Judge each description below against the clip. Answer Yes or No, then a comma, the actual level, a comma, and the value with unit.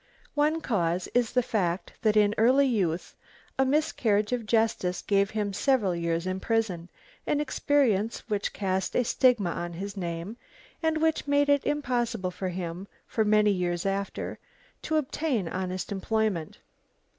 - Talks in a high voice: Yes, high, 210 Hz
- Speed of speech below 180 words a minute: Yes, average, 150 wpm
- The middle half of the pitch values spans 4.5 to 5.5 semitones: Yes, average, 5.2 semitones